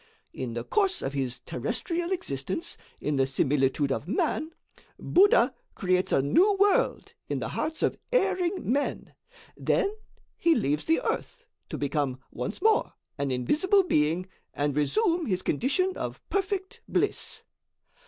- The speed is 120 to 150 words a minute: Yes, average, 140 wpm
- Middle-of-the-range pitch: No, high, 235 Hz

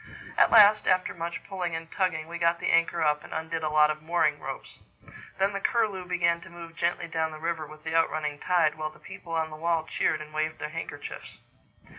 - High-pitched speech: No, medium, 165 Hz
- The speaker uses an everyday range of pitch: No, narrow, 1.8 semitones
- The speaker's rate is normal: No, fast, 225 wpm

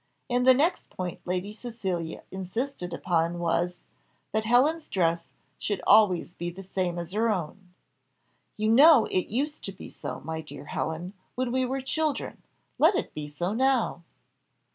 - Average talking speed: Yes, average, 160 wpm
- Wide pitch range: Yes, wide, 6.3 semitones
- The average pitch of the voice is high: Yes, high, 195 Hz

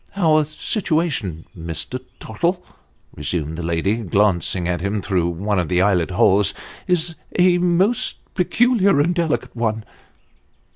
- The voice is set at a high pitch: No, low, 105 Hz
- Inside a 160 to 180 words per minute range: No, slow, 135 wpm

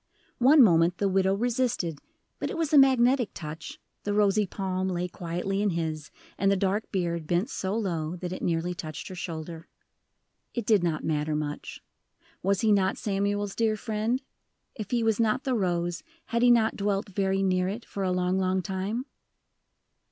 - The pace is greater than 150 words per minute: Yes, average, 180 wpm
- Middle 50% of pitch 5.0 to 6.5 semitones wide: No, average, 3.6 semitones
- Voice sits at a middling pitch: No, high, 195 Hz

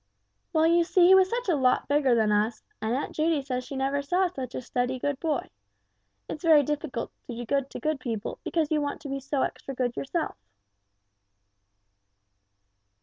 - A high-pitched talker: Yes, very high, 280 Hz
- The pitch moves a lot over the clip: No, average, 3.8 semitones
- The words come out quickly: No, average, 190 wpm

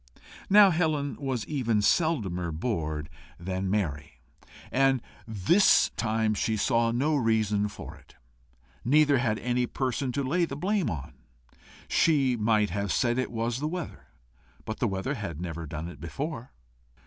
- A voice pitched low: Yes, low, 115 Hz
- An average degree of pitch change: No, wide, 6.0 semitones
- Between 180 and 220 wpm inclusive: No, average, 150 wpm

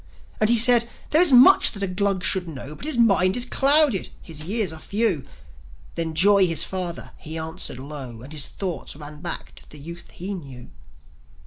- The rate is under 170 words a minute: No, average, 195 wpm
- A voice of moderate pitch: Yes, medium, 180 Hz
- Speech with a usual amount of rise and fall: No, wide, 5.7 semitones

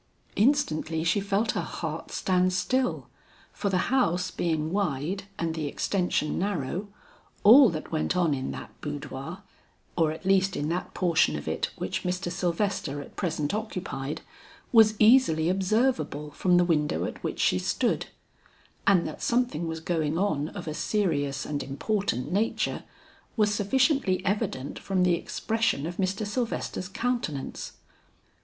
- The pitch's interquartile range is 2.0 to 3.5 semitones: No, average, 4.7 semitones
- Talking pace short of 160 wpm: Yes, average, 145 wpm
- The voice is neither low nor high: Yes, medium, 180 Hz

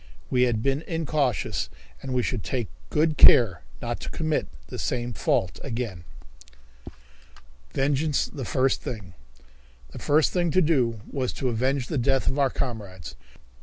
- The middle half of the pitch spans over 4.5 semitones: No, average, 3.8 semitones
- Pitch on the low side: Yes, low, 130 Hz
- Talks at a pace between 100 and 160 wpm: Yes, average, 150 wpm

